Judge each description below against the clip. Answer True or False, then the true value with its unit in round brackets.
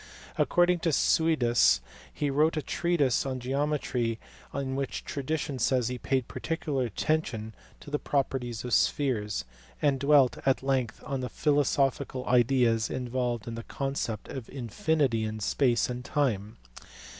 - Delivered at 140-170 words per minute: True (145 wpm)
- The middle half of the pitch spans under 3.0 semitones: False (3.4 semitones)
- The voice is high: False (130 Hz)